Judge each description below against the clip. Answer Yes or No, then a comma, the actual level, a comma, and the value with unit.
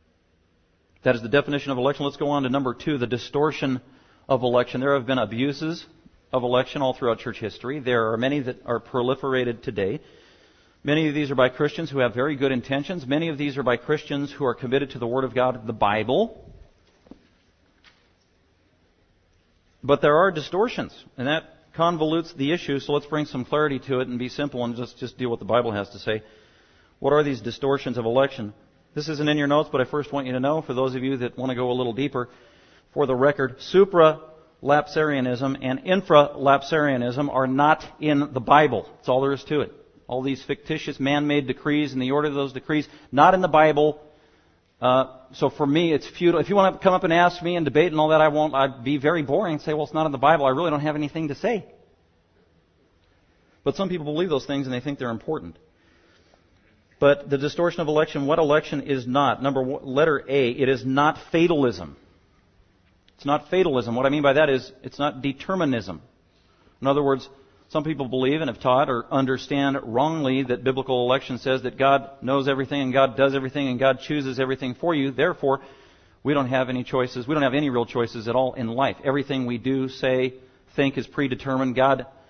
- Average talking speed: No, fast, 210 wpm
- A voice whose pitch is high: No, low, 135 Hz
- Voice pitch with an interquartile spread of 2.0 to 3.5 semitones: Yes, average, 3.0 semitones